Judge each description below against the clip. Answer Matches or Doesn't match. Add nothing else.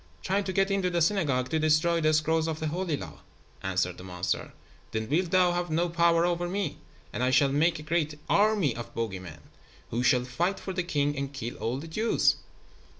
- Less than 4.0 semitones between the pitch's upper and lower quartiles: Doesn't match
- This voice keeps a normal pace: Doesn't match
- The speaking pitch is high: Doesn't match